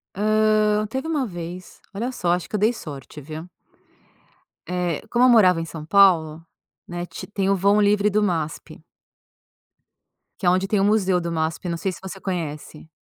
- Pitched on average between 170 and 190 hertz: Yes, medium, 185 Hz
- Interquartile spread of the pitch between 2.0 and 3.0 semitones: No, average, 3.9 semitones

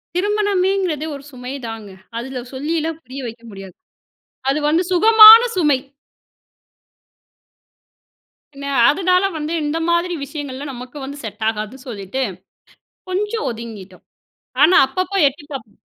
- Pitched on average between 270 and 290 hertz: Yes, very high, 285 Hz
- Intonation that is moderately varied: No, wide, 7.0 semitones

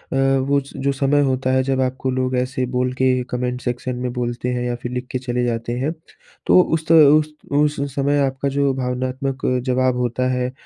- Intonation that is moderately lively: No, narrow, 1.5 semitones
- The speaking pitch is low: Yes, low, 130 Hz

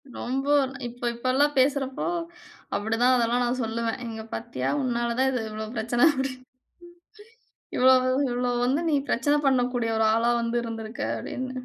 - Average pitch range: No, narrow, 1.9 semitones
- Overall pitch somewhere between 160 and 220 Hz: No, high, 245 Hz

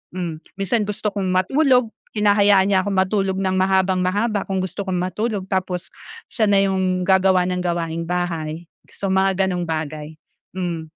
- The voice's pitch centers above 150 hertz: Yes, high, 190 Hz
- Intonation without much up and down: Yes, narrow, 1.9 semitones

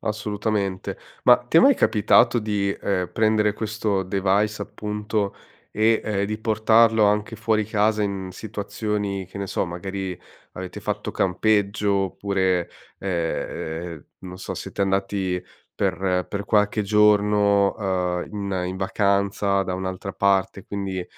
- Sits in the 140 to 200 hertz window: No, low, 100 Hz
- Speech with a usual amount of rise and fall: No, narrow, 1.9 semitones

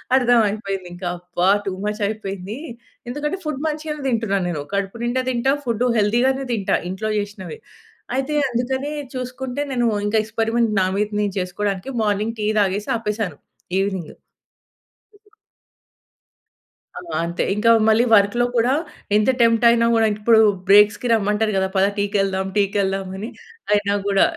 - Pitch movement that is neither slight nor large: Yes, average, 3.3 semitones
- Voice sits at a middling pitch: No, high, 210 Hz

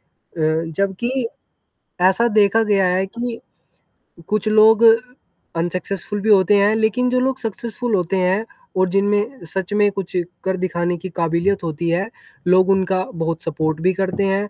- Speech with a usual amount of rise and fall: Yes, average, 3.2 semitones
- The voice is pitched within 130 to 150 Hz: No, high, 195 Hz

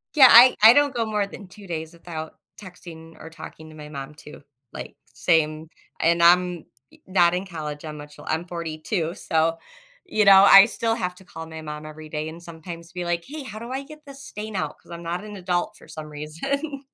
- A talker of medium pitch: Yes, medium, 170 Hz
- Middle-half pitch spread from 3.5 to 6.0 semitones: Yes, average, 4.7 semitones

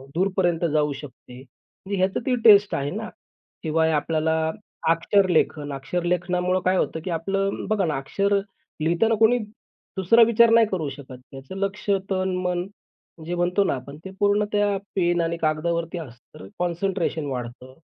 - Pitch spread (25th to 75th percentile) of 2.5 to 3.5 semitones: No, average, 4.1 semitones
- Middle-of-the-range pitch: Yes, medium, 175 Hz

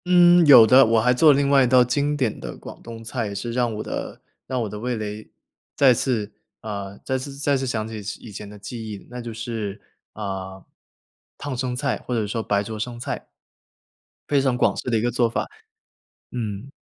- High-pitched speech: No, low, 120 Hz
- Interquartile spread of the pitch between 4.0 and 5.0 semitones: No, average, 3.3 semitones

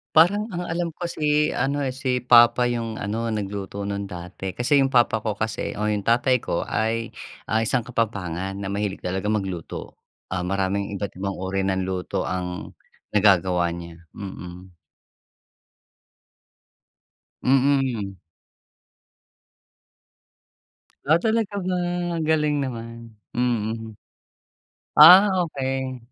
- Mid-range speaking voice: No, low, 110 Hz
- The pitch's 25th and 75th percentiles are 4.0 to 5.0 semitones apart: No, wide, 5.4 semitones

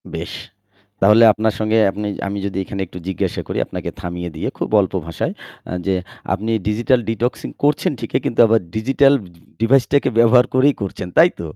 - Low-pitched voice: Yes, low, 110 Hz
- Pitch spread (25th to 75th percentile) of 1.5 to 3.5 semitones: No, average, 4.2 semitones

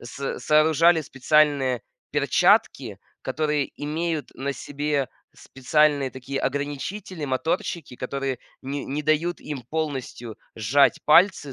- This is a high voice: No, medium, 145 Hz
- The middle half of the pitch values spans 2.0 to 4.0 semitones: Yes, narrow, 2.4 semitones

